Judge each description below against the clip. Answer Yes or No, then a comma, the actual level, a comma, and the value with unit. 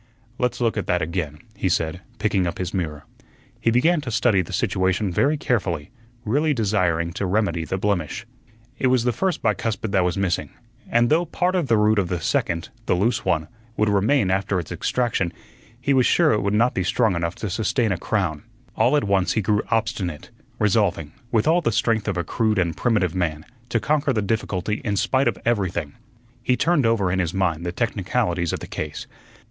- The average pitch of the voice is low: Yes, low, 100 Hz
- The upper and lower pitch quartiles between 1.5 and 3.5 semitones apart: No, average, 4.7 semitones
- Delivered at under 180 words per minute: No, average, 200 wpm